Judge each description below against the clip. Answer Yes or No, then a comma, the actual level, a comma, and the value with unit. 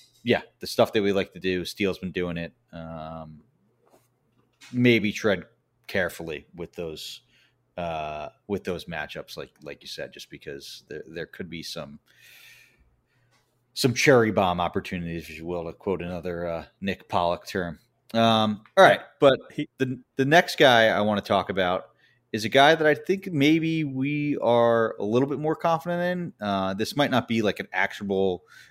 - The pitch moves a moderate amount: No, wide, 7.5 semitones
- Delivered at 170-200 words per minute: Yes, average, 175 wpm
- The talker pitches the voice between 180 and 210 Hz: No, low, 110 Hz